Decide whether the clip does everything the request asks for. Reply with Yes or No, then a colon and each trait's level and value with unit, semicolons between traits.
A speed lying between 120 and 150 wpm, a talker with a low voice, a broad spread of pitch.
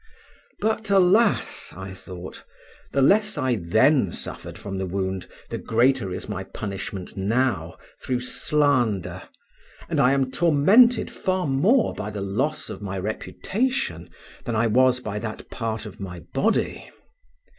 Yes: average, 145 wpm; low, 115 Hz; wide, 7.5 semitones